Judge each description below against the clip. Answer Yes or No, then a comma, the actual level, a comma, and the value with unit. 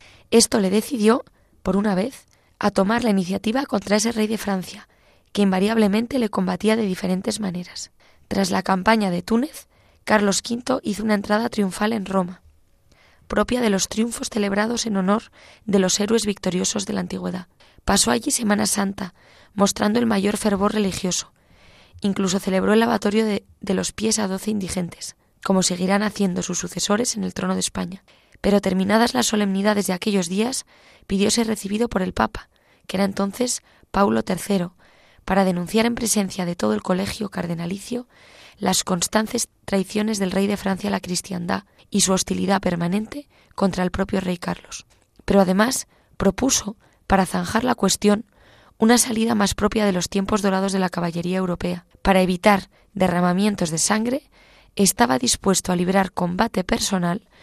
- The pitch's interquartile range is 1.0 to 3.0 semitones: Yes, narrow, 2.6 semitones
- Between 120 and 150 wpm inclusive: No, average, 160 wpm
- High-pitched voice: Yes, high, 200 Hz